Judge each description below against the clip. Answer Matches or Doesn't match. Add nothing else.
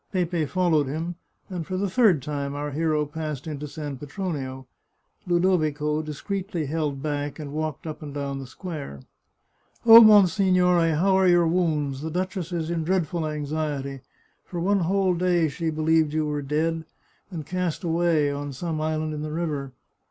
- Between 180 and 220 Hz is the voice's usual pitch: Doesn't match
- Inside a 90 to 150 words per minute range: Doesn't match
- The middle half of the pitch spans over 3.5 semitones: Doesn't match